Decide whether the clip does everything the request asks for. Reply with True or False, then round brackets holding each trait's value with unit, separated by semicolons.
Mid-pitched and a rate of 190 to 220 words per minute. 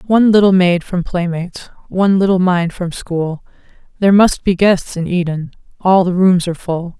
False (180 Hz; 180 wpm)